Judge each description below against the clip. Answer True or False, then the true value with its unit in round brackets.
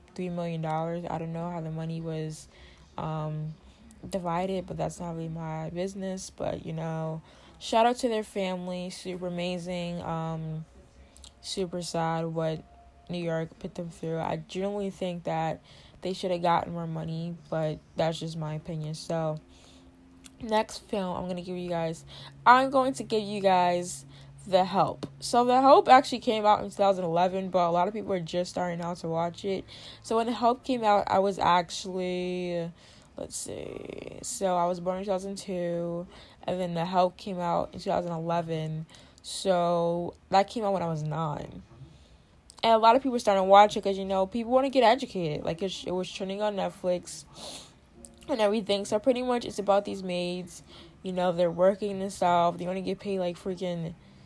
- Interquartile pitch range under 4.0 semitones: True (3.2 semitones)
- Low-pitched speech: False (180 Hz)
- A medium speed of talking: True (180 wpm)